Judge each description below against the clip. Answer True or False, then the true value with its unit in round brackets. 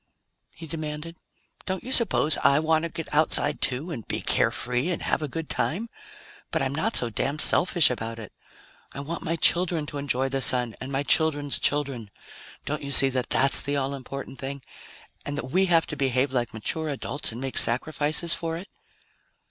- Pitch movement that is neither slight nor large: True (3.5 semitones)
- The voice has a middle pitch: True (145 Hz)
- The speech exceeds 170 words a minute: True (190 wpm)